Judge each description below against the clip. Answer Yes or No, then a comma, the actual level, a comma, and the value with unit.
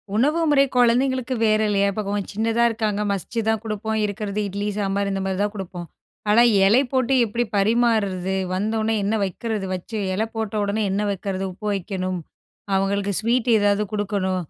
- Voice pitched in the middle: No, high, 210 Hz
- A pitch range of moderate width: No, narrow, 2.3 semitones